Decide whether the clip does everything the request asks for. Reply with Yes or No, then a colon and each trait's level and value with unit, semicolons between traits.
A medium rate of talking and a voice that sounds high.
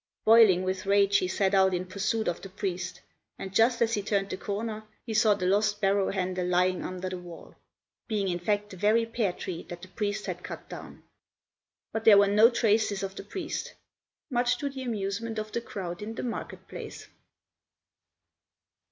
Yes: average, 190 wpm; high, 200 Hz